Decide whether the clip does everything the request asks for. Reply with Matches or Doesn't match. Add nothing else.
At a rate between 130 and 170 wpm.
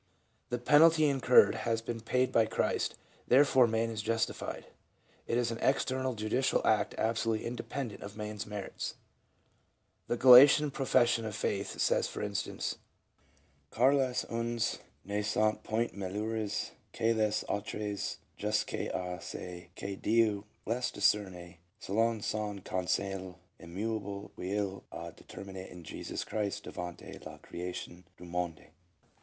Matches